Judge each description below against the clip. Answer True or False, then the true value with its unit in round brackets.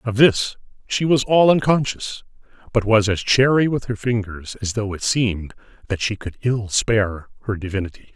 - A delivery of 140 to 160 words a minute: False (175 wpm)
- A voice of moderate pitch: False (110 Hz)